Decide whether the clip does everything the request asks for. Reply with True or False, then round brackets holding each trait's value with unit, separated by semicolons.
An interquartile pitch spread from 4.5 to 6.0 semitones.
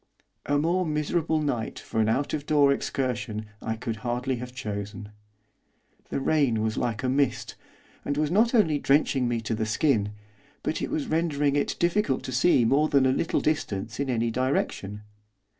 True (4.9 semitones)